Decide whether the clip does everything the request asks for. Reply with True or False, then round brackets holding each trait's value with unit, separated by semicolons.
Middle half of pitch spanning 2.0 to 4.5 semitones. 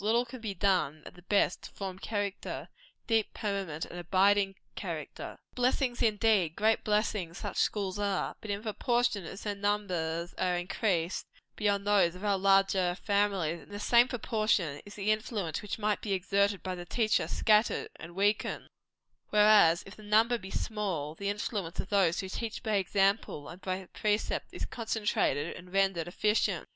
True (2.7 semitones)